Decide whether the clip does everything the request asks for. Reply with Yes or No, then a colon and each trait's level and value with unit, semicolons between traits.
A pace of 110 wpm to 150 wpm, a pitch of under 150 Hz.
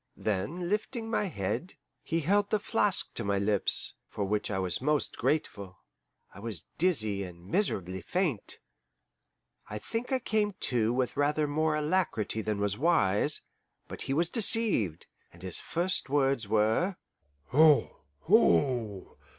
Yes: average, 140 wpm; low, 135 Hz